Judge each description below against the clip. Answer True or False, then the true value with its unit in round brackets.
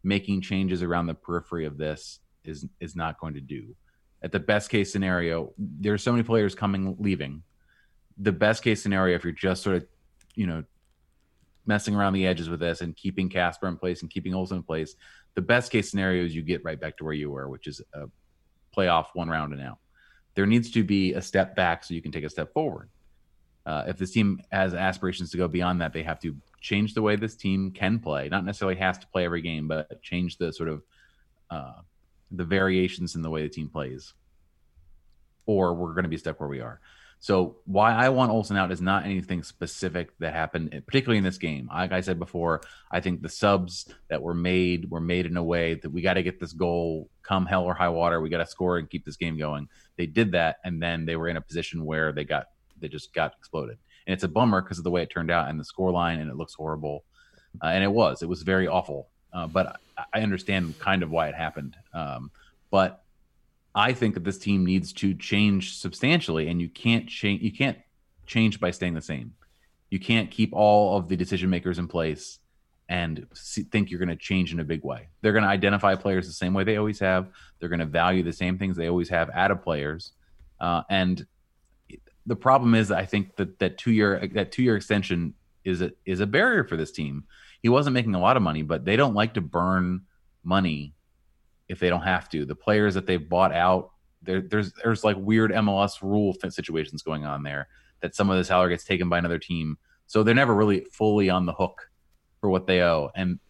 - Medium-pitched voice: False (90 Hz)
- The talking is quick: True (225 wpm)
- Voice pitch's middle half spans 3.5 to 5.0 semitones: False (3.1 semitones)